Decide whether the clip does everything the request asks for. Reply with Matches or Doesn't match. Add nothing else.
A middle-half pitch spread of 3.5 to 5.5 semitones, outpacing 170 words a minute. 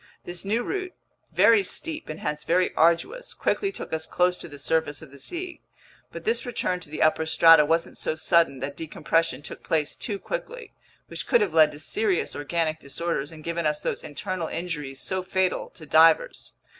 Matches